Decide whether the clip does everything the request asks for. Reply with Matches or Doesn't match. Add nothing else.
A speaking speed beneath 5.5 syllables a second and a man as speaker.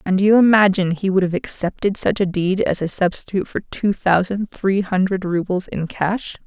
Doesn't match